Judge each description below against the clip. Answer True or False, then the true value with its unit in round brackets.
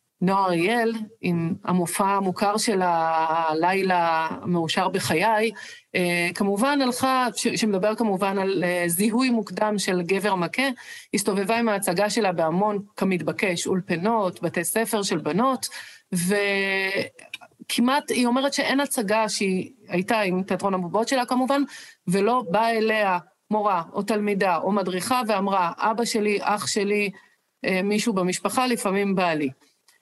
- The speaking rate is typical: True (120 wpm)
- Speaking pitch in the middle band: False (205 Hz)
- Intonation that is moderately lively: True (3.8 semitones)